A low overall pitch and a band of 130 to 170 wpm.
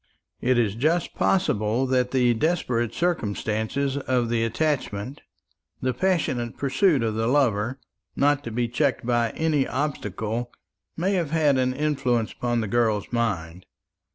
Yes: low, 125 Hz; average, 140 wpm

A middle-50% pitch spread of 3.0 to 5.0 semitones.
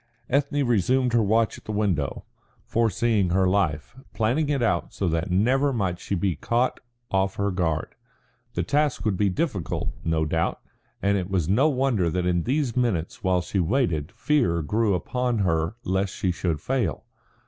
No: wide, 5.6 semitones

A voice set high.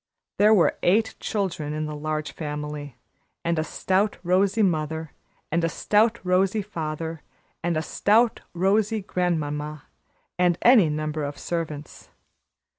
No: medium, 165 Hz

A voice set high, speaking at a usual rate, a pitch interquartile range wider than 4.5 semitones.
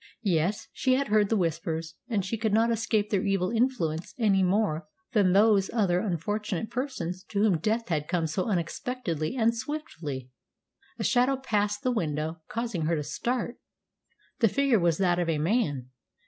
Yes: high, 200 Hz; average, 170 wpm; wide, 5.4 semitones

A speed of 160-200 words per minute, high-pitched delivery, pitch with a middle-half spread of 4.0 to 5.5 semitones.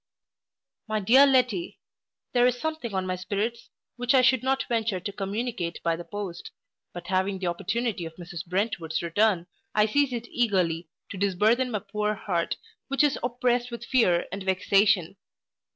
Yes: average, 165 wpm; high, 205 Hz; average, 4.8 semitones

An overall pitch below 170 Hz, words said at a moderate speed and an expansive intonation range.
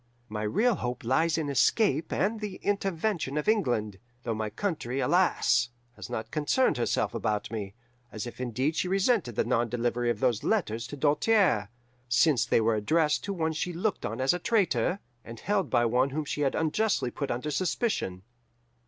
Yes: medium, 140 Hz; average, 180 wpm; wide, 7.4 semitones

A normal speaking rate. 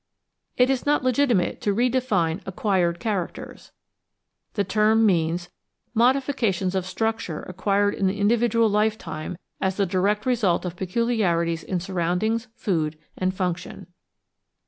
No: slow, 130 wpm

